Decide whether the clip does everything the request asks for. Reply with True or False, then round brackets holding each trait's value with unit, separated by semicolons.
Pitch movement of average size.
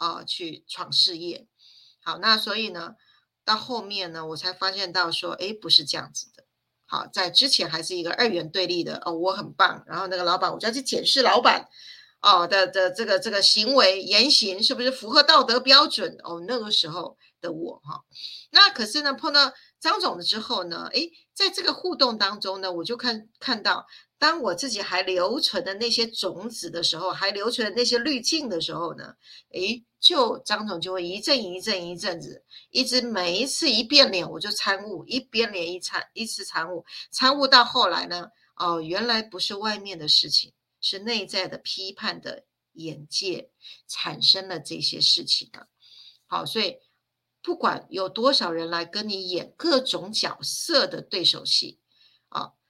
False (5.8 semitones)